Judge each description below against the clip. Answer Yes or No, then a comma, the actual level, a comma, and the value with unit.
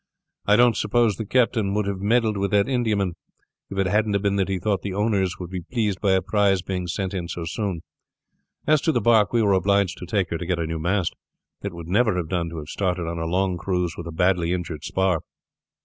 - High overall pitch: No, very low, 95 Hz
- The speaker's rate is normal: No, fast, 240 wpm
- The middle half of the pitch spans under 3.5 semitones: Yes, average, 2.8 semitones